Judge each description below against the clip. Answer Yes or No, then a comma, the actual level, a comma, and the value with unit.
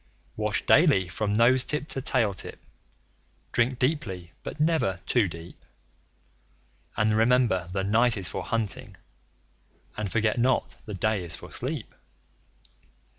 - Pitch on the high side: No, low, 110 Hz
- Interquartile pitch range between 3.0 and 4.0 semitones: No, average, 4.7 semitones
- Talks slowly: Yes, slow, 130 wpm